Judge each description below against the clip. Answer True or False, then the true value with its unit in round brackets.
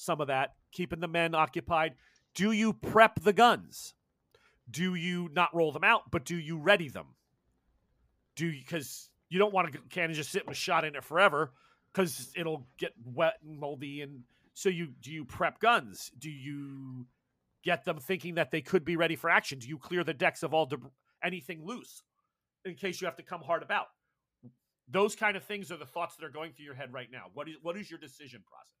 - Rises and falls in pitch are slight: False (3.7 semitones)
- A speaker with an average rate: False (215 wpm)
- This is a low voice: False (165 Hz)